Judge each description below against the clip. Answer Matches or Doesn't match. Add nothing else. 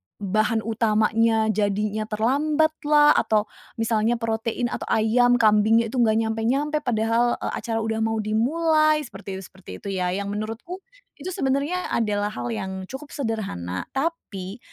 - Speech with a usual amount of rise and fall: Matches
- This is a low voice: Doesn't match